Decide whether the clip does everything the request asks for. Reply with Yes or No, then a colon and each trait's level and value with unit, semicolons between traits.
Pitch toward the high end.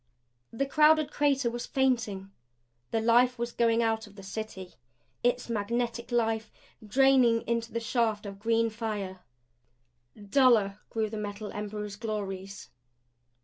Yes: high, 225 Hz